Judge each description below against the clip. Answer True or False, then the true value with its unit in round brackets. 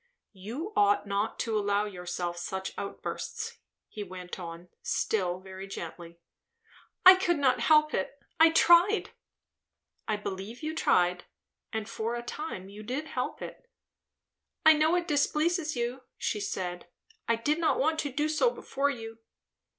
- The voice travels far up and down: True (8.2 semitones)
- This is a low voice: False (230 Hz)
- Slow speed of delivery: False (150 wpm)